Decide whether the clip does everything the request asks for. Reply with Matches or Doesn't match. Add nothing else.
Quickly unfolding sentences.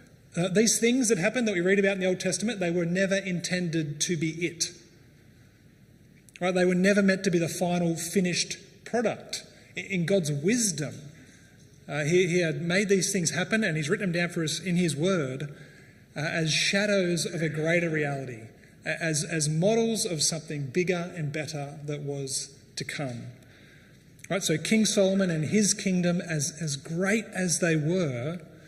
Doesn't match